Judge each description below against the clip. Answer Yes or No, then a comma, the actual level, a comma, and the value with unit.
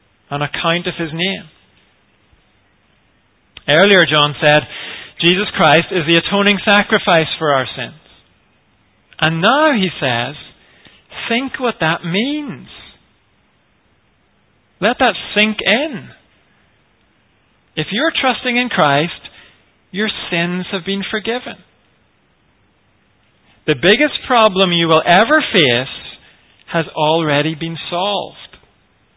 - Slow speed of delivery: Yes, slow, 105 wpm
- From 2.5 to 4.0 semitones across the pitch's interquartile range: No, wide, 5.5 semitones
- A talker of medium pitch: Yes, medium, 175 Hz